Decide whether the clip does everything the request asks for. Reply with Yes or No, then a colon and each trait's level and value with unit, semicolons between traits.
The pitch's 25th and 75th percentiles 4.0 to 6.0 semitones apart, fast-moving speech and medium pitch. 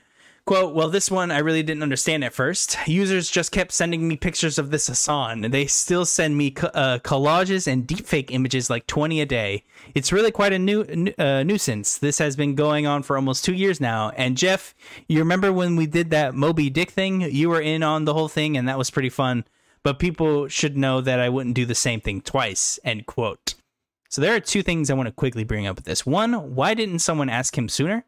Yes: average, 4.9 semitones; fast, 230 wpm; medium, 150 Hz